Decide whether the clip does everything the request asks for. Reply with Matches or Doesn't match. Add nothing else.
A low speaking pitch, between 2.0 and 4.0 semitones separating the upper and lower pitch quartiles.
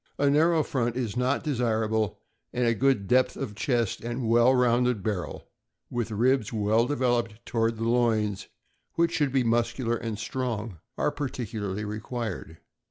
Matches